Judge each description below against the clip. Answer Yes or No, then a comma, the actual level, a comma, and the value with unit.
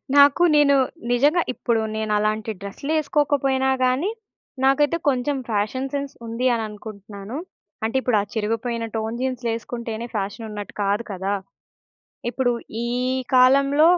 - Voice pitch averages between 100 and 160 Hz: No, high, 240 Hz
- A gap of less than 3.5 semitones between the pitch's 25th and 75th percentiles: No, average, 4.1 semitones